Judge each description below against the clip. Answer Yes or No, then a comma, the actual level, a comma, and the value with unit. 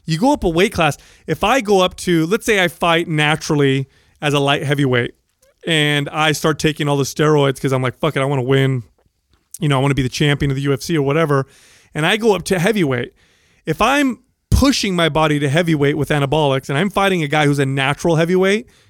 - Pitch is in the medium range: Yes, medium, 155 Hz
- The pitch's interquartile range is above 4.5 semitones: No, average, 3.9 semitones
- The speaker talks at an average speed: No, fast, 225 wpm